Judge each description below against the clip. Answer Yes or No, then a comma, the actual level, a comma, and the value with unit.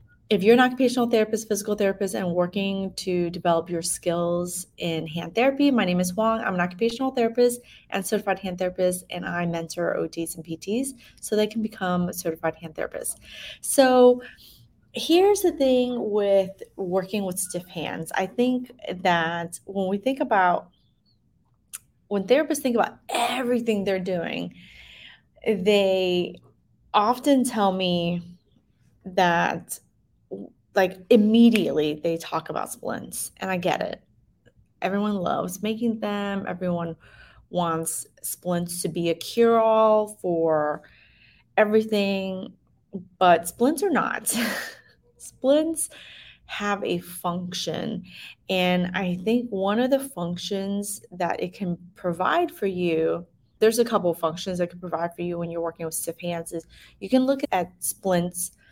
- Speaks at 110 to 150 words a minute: Yes, average, 140 wpm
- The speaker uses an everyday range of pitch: Yes, average, 4.2 semitones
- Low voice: No, high, 190 Hz